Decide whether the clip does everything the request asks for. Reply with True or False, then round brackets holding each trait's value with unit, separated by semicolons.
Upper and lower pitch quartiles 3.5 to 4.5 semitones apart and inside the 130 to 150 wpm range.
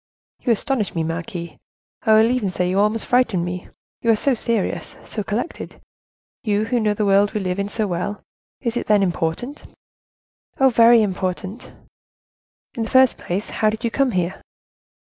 False (4.0 semitones; 170 wpm)